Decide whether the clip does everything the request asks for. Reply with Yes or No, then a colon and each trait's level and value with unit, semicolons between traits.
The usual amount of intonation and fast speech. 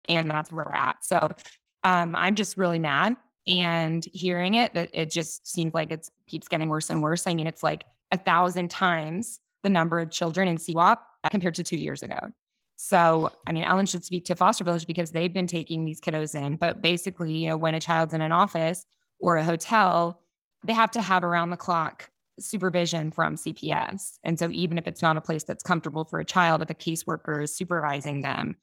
No: narrow, 2.0 semitones; fast, 210 wpm